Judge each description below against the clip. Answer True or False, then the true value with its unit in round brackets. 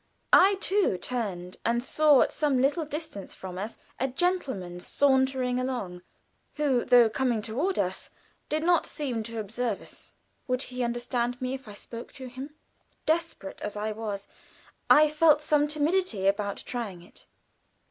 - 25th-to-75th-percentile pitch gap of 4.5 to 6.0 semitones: True (5.5 semitones)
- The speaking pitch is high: True (250 Hz)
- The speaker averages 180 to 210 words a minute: False (155 wpm)